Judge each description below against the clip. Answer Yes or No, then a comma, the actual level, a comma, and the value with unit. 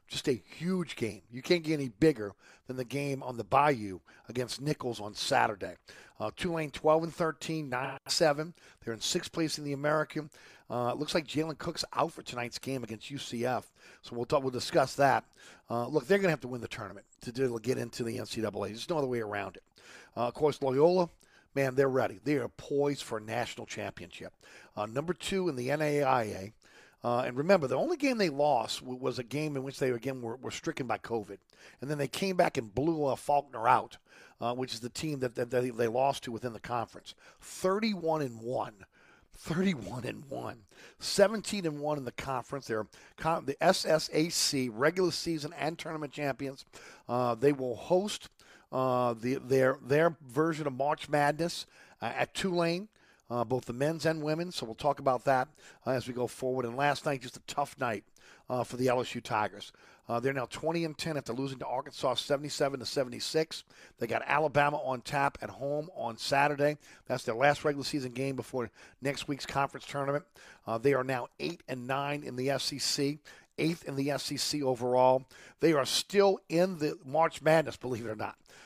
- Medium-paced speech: Yes, average, 195 wpm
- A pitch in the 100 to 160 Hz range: Yes, medium, 140 Hz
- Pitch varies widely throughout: No, average, 3.8 semitones